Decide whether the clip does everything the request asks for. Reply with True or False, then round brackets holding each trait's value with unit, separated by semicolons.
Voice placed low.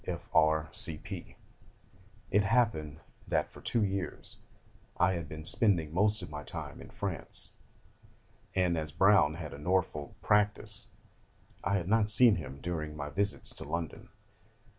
True (85 Hz)